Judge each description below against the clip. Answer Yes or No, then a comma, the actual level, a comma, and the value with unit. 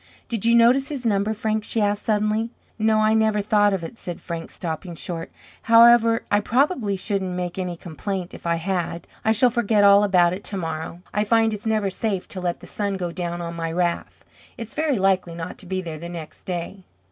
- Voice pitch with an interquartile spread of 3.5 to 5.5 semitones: Yes, average, 3.9 semitones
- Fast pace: Yes, fast, 210 wpm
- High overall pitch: Yes, high, 200 Hz